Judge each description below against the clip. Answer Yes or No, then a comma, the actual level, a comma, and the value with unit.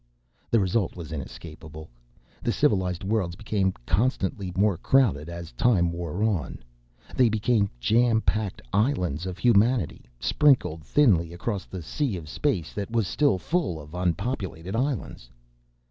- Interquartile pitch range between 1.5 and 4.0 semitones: No, average, 5.1 semitones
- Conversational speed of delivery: No, slow, 130 wpm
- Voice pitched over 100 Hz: No, very low, 95 Hz